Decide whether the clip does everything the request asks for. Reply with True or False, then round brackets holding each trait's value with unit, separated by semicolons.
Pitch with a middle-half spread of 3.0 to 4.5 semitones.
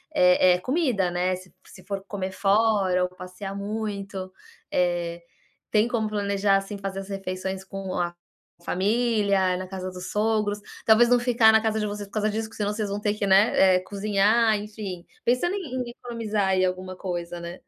False (2.6 semitones)